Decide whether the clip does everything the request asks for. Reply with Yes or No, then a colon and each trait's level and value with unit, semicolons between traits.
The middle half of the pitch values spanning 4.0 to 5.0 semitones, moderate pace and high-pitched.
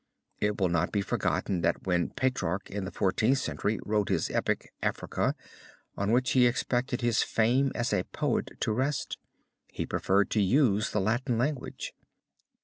No: average, 4.3 semitones; average, 160 wpm; low, 110 Hz